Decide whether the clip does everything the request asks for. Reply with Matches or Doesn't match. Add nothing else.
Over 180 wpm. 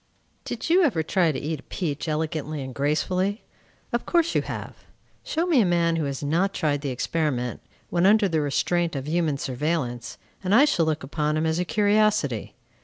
Matches